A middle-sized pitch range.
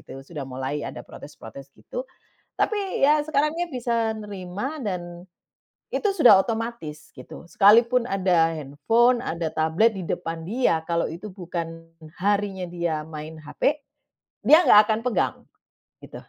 No: wide, 6.5 semitones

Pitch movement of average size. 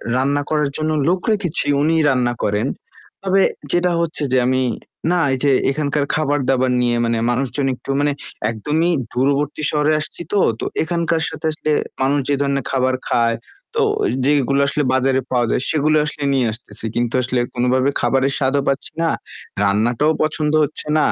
Yes: average, 3.1 semitones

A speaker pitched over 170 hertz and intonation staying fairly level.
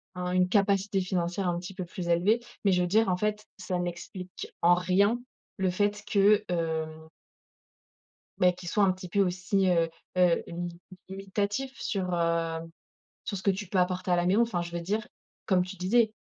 Yes: medium, 185 Hz; narrow, 2.3 semitones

